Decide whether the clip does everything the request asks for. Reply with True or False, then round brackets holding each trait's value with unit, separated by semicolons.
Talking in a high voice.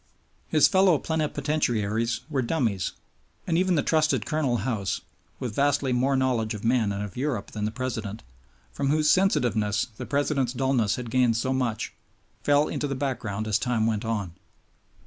False (125 Hz)